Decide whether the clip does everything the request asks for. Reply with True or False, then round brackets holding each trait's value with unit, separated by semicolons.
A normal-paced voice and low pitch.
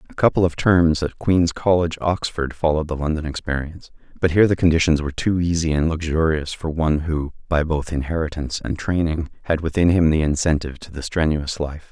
True (190 wpm; 80 Hz)